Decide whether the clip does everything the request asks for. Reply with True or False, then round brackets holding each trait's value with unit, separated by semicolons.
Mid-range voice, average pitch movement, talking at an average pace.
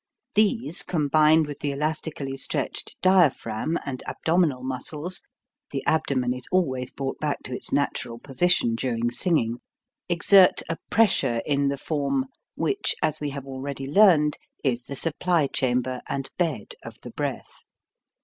True (145 Hz; 4.0 semitones; 145 wpm)